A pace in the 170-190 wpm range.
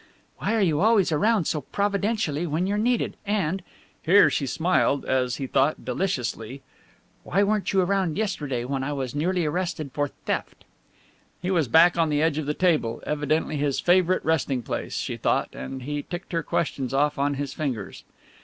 Yes: average, 180 wpm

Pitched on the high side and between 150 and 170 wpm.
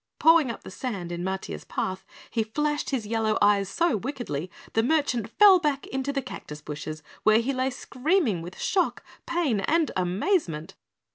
Yes: high, 230 Hz; average, 165 wpm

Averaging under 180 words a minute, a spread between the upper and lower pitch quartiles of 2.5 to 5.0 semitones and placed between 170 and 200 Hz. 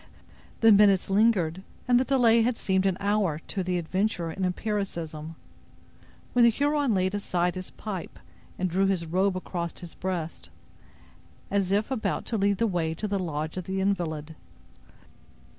Yes: average, 160 wpm; average, 3.3 semitones; high, 190 Hz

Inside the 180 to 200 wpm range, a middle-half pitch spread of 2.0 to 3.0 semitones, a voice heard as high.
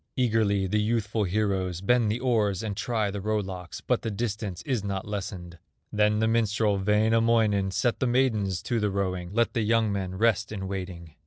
No: average, 185 wpm; average, 2.7 semitones; low, 105 Hz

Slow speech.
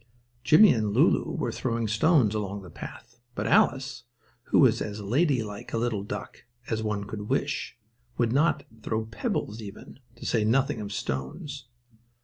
No: average, 155 wpm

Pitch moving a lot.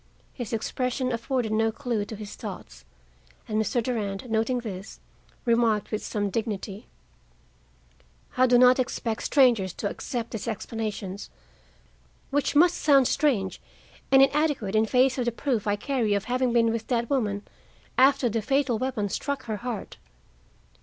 No: average, 3.2 semitones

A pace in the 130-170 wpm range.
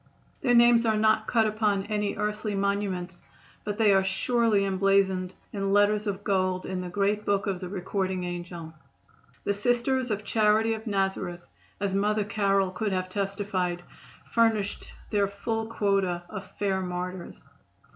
Yes: average, 150 wpm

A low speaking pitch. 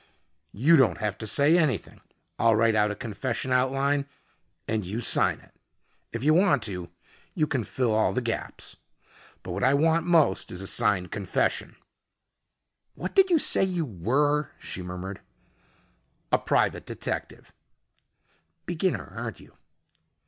Yes: low, 120 Hz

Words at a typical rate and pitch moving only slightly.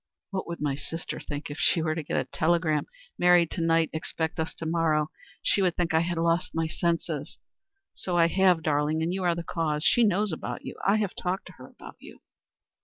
No: fast, 220 wpm; narrow, 2.0 semitones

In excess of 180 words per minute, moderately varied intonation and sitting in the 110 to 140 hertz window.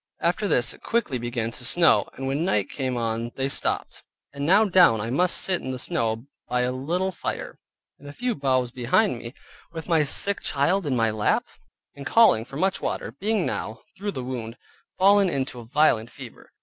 No: average, 200 wpm; wide, 7.1 semitones; low, 135 Hz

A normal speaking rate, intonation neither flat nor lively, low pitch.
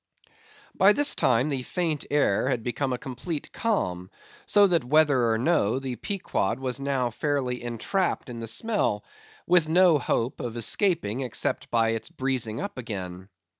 No: average, 160 wpm; wide, 5.9 semitones; low, 130 Hz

